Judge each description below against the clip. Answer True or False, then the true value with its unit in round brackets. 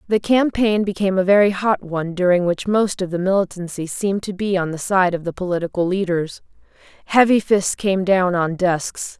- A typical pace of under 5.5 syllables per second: True (5.3 syllables/s)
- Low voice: False (190 Hz)